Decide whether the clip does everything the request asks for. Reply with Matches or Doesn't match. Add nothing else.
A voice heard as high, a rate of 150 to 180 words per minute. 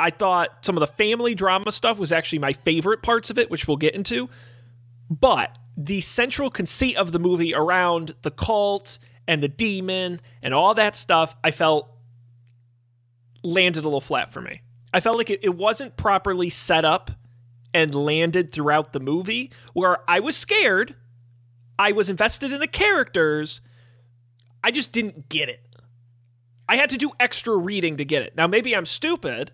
Doesn't match